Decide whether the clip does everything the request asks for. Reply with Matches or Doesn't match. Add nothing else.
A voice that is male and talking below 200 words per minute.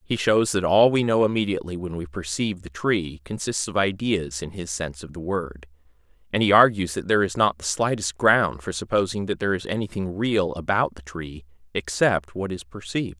Doesn't match